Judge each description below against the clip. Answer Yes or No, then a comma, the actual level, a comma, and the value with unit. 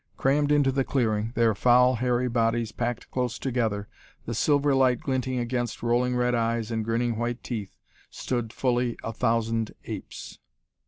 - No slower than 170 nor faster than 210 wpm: No, average, 155 wpm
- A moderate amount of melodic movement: No, narrow, 1.8 semitones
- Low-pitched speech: Yes, low, 120 Hz